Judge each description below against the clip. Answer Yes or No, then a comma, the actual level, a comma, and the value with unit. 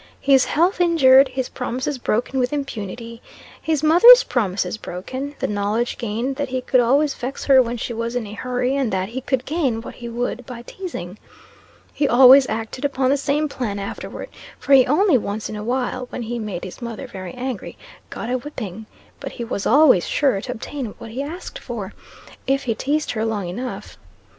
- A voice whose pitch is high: Yes, very high, 250 Hz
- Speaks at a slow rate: No, average, 195 wpm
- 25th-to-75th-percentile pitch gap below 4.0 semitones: Yes, average, 3.6 semitones